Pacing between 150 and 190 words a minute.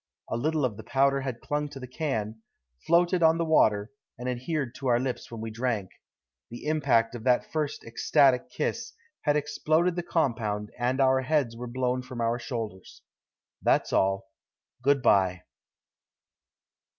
Yes: average, 160 wpm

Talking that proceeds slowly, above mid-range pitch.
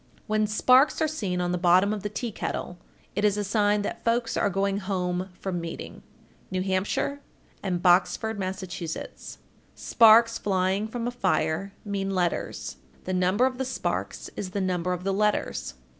No: average, 175 wpm; high, 195 Hz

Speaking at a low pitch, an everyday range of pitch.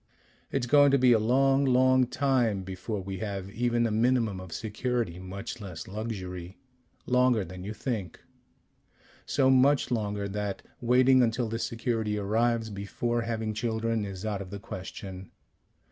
Yes: low, 110 Hz; average, 3.8 semitones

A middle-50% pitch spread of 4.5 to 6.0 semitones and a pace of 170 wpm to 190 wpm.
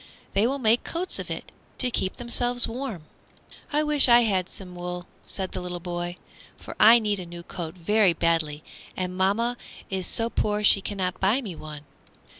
Yes: average, 4.9 semitones; average, 180 wpm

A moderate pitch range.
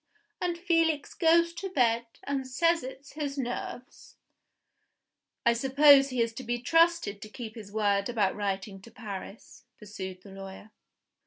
No: wide, 6.0 semitones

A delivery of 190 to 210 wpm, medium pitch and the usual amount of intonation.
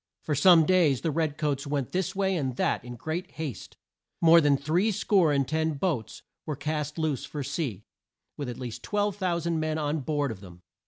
Yes: average, 195 wpm; medium, 150 Hz; average, 3.4 semitones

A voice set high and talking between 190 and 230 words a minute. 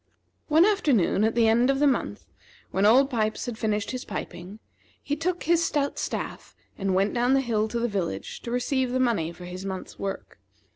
Yes: high, 235 Hz; average, 200 wpm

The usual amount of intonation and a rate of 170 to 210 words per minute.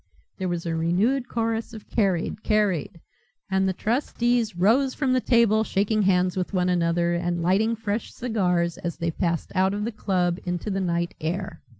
Yes: average, 4.1 semitones; average, 180 wpm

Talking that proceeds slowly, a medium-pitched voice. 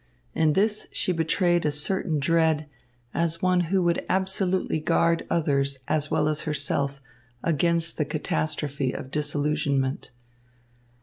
Yes: slow, 125 wpm; medium, 155 Hz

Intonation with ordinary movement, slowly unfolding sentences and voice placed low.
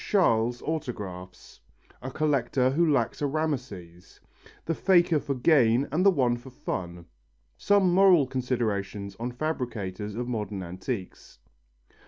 No: wide, 6.8 semitones; slow, 125 wpm; low, 125 Hz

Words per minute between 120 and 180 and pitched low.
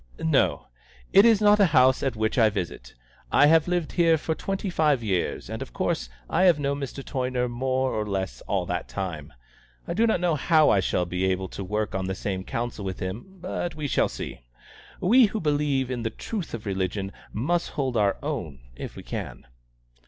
No: fast, 205 wpm; low, 130 Hz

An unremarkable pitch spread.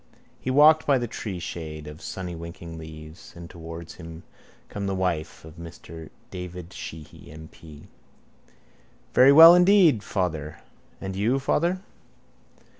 No: wide, 6.8 semitones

